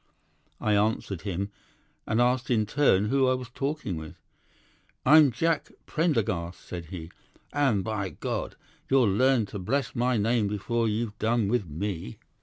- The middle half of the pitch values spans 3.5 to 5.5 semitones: Yes, average, 4.5 semitones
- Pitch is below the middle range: Yes, low, 110 Hz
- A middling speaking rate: Yes, average, 150 wpm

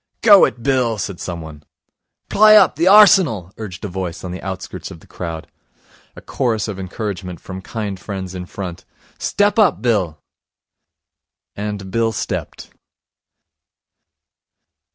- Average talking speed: No, slow, 130 wpm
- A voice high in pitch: No, low, 100 Hz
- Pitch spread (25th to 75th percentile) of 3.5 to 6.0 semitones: Yes, average, 4.4 semitones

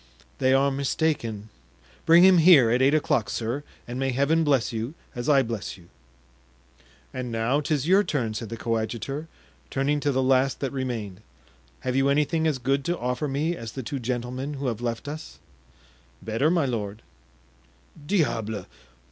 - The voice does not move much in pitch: No, average, 4.1 semitones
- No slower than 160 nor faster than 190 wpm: Yes, average, 165 wpm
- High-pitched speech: No, low, 130 Hz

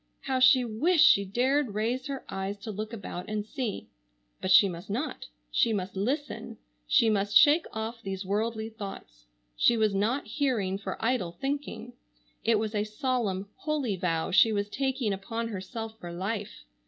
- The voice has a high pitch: Yes, high, 220 Hz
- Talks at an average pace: Yes, average, 165 wpm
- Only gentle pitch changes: No, average, 4.2 semitones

